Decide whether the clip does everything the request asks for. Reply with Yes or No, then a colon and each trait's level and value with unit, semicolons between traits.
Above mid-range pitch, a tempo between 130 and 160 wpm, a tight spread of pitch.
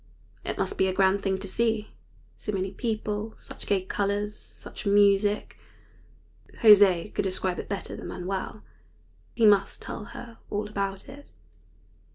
Yes: high, 200 Hz; average, 150 wpm; narrow, 1.6 semitones